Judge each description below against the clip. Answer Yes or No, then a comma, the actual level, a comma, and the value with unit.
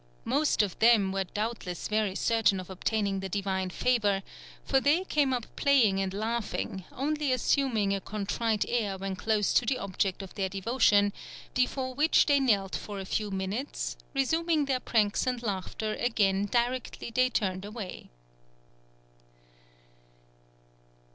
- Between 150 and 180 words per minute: No, average, 140 wpm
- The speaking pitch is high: Yes, high, 215 Hz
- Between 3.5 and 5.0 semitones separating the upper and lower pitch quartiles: Yes, average, 4.5 semitones